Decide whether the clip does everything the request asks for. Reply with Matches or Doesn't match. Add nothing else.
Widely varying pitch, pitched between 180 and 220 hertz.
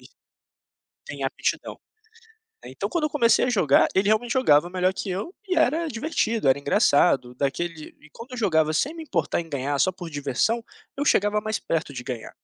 Matches